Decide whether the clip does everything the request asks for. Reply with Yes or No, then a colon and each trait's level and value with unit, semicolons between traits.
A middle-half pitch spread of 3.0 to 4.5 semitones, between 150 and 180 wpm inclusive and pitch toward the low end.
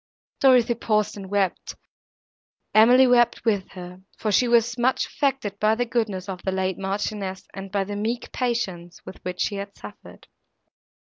No: average, 3.7 semitones; average, 165 wpm; high, 205 Hz